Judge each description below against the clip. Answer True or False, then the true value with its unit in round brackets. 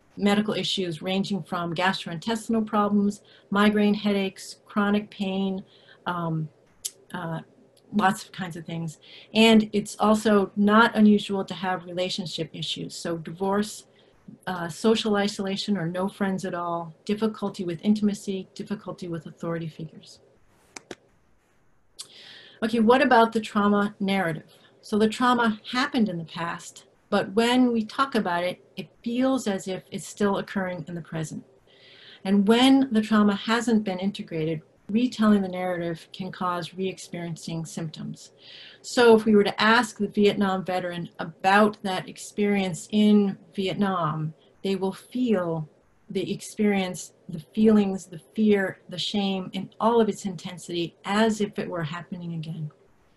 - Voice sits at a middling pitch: False (195 Hz)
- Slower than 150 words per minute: True (140 wpm)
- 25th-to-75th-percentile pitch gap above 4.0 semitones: False (3.1 semitones)